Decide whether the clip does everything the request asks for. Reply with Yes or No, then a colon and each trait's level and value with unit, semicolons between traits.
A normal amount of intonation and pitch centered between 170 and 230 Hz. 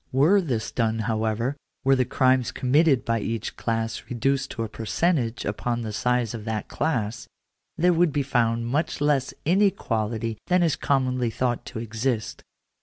No: average, 3.5 semitones; low, 125 Hz